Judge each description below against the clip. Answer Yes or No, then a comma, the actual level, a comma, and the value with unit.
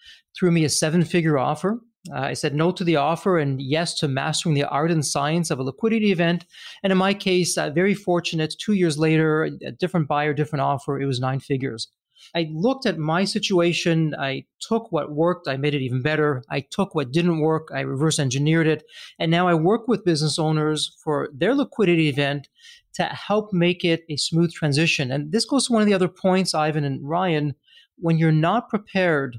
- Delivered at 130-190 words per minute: No, fast, 205 wpm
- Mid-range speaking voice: Yes, medium, 165 Hz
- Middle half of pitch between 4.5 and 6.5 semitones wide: No, average, 3.6 semitones